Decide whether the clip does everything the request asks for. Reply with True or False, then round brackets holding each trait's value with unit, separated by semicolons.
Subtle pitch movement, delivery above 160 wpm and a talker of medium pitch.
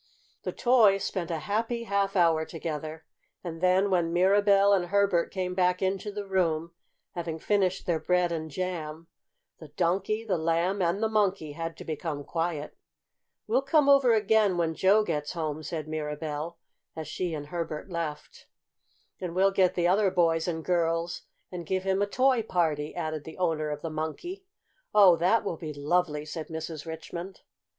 False (3.4 semitones; 170 wpm; 175 Hz)